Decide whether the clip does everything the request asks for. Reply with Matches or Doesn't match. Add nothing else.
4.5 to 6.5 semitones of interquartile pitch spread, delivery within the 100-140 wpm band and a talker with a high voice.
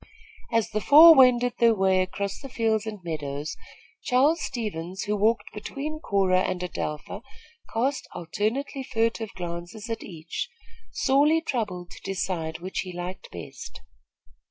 Matches